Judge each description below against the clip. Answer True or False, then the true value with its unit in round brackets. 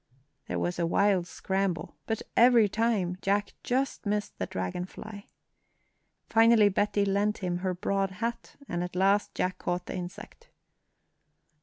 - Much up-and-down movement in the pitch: False (2.7 semitones)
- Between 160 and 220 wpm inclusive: False (145 wpm)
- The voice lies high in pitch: True (195 Hz)